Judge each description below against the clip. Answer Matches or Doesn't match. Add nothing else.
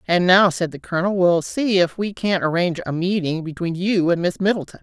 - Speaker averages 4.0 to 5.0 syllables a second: Doesn't match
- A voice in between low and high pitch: Matches